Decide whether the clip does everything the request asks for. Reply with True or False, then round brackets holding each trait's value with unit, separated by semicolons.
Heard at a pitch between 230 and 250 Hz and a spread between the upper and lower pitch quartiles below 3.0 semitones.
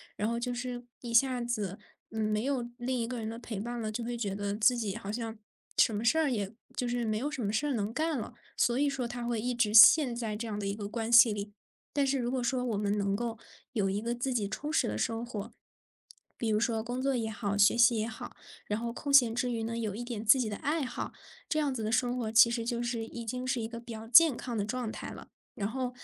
True (235 Hz; 2.4 semitones)